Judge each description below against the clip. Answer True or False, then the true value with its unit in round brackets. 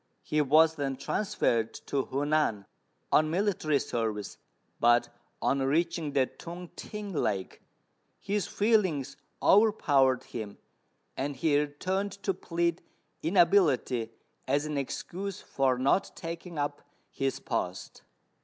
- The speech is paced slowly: True (115 wpm)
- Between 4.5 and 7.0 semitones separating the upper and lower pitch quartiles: True (4.8 semitones)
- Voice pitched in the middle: True (150 Hz)